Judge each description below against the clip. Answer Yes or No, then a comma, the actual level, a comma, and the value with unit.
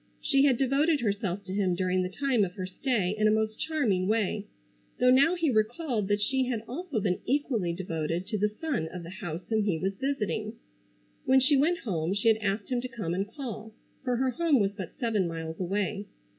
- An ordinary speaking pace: No, fast, 210 wpm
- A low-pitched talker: No, high, 215 Hz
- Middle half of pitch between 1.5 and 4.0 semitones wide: No, wide, 5.5 semitones